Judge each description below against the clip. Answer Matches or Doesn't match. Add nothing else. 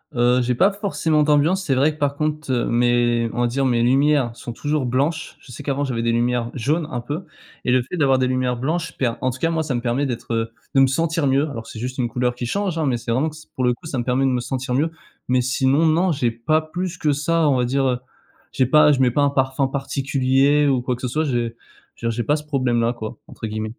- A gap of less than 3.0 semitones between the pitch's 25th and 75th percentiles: Doesn't match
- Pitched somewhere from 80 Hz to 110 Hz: Doesn't match